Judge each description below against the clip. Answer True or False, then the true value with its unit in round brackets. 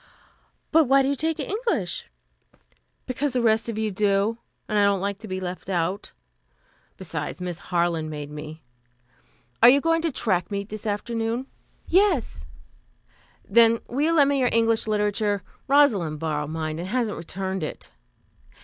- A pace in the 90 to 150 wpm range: False (160 wpm)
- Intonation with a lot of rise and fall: True (5.8 semitones)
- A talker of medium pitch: False (210 Hz)